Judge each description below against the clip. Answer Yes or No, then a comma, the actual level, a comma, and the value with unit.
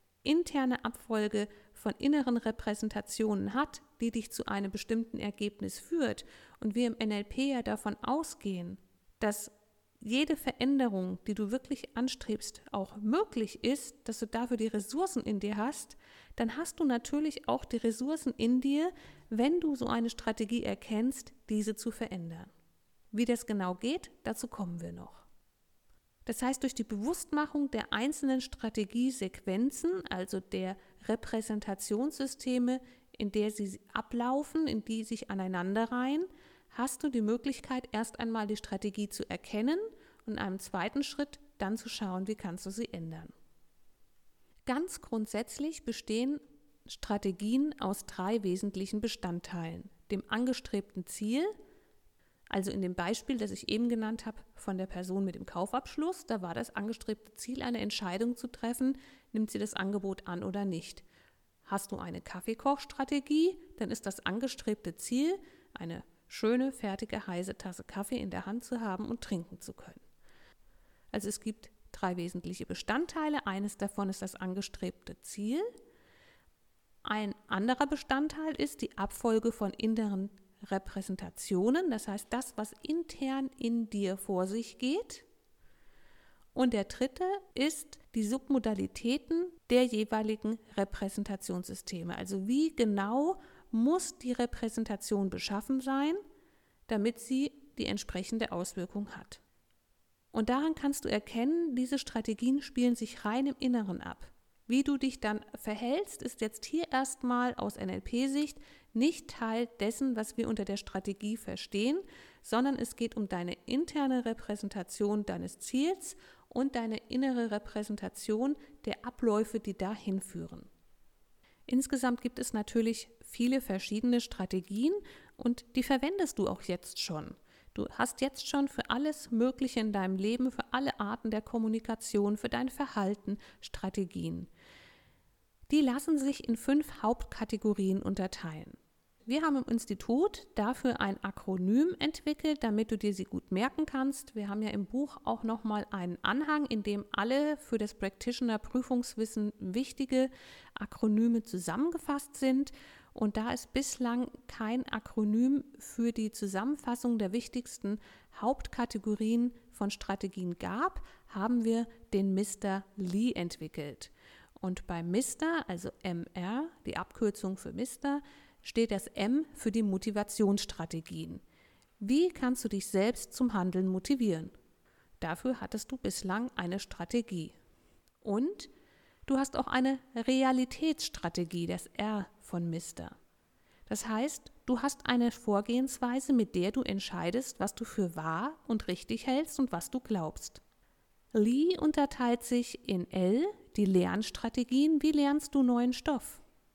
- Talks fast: No, average, 135 wpm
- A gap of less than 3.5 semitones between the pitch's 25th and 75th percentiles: No, average, 4.8 semitones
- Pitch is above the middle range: Yes, high, 230 Hz